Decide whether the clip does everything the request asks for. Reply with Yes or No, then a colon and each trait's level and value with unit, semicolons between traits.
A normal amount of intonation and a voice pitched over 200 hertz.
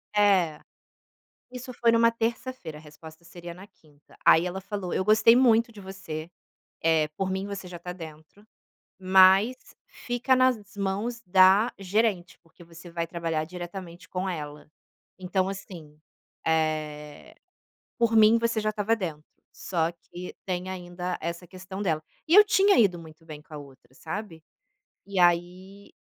No: average, 4.1 semitones; medium, 185 Hz